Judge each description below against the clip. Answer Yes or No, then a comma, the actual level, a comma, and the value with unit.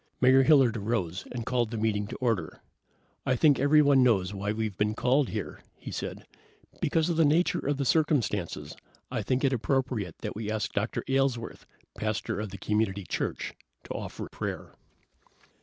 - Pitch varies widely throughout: No, average, 4.3 semitones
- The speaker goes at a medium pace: Yes, average, 170 wpm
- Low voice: Yes, low, 115 Hz